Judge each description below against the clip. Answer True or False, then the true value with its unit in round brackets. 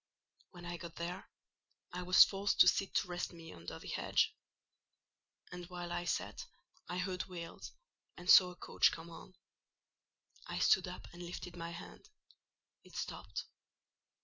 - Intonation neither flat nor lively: False (1.1 semitones)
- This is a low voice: False (175 Hz)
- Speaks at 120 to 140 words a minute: False (155 wpm)